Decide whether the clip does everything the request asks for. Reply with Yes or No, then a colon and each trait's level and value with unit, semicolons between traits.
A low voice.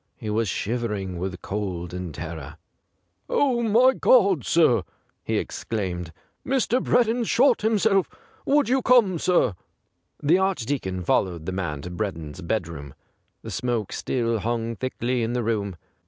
Yes: low, 115 Hz